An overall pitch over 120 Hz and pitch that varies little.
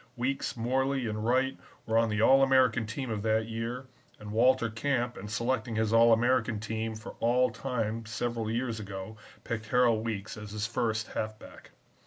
No: low, 115 Hz; narrow, 2.3 semitones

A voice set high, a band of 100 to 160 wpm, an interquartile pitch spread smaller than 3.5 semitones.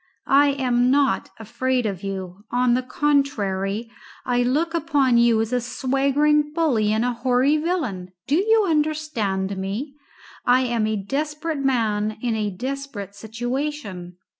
No: very high, 250 Hz; average, 140 wpm; average, 5.0 semitones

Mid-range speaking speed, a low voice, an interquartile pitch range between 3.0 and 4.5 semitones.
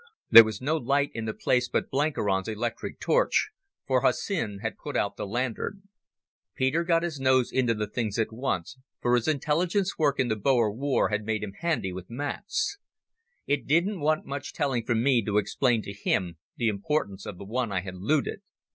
No: average, 190 wpm; low, 125 Hz; wide, 5.5 semitones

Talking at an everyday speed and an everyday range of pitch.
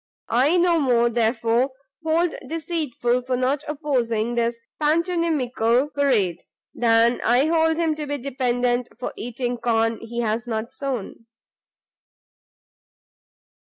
No: slow, 120 wpm; average, 4.3 semitones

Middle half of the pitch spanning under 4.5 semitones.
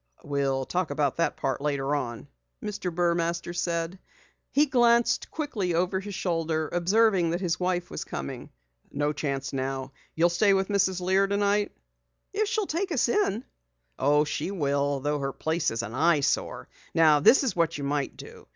No: wide, 5.5 semitones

